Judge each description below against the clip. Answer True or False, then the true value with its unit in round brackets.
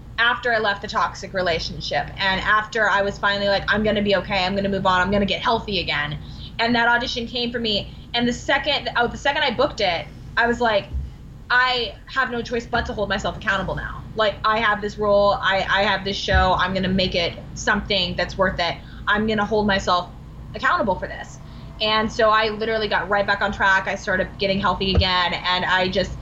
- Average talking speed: False (215 wpm)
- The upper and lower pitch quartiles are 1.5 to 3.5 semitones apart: True (3.2 semitones)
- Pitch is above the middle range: True (200 Hz)